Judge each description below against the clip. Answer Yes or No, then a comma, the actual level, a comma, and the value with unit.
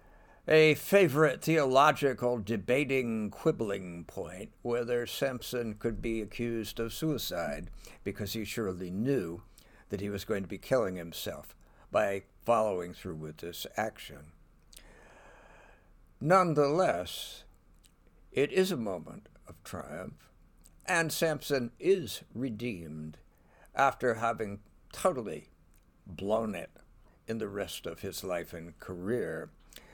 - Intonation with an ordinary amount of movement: No, wide, 7.0 semitones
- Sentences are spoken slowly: Yes, slow, 110 wpm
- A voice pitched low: Yes, low, 110 Hz